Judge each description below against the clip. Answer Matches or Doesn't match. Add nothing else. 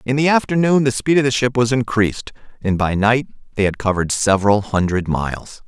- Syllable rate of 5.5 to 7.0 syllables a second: Matches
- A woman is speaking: Doesn't match